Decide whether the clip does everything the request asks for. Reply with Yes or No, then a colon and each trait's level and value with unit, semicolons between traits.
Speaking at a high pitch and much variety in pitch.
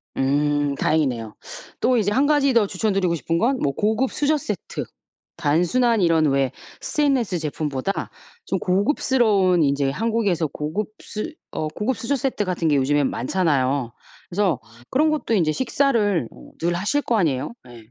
No: medium, 180 Hz; wide, 7.8 semitones